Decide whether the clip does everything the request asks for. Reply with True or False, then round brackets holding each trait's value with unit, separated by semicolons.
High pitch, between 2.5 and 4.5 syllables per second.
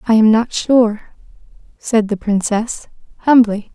True (220 Hz; 3.9 syllables/s)